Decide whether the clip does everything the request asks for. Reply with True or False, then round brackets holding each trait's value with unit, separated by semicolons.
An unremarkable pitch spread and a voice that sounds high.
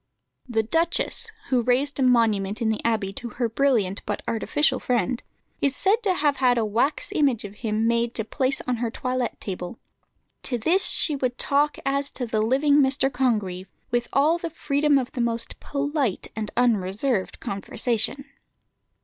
True (4.0 semitones; 245 Hz)